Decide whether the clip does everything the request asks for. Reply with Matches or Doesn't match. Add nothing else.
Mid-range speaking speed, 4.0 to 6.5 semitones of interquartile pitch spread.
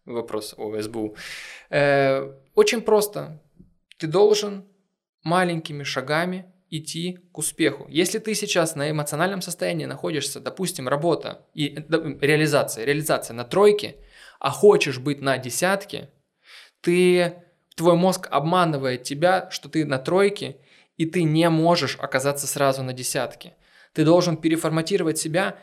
Matches